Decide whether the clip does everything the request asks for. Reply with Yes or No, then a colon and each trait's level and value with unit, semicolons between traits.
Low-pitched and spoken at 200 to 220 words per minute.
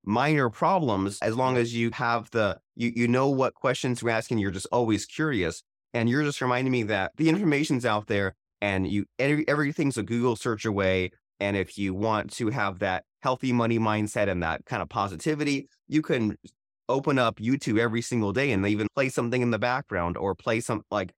Yes: low, 115 Hz; fast, 205 wpm